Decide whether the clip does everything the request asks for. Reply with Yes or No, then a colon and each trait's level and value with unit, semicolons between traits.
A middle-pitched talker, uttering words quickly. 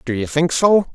Yes: medium, 155 Hz; fast, 255 wpm